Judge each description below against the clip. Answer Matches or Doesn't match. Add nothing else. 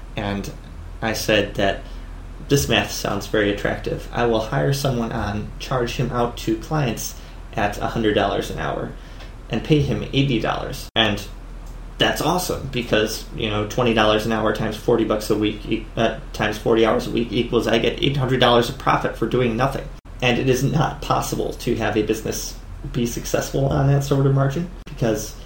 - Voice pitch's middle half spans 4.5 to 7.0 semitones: Doesn't match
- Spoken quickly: Doesn't match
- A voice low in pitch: Matches